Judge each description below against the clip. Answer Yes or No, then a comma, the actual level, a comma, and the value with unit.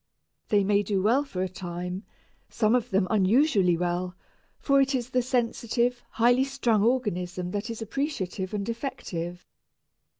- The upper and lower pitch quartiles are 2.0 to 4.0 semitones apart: No, average, 5.1 semitones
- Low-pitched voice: No, high, 215 Hz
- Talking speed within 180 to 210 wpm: No, average, 145 wpm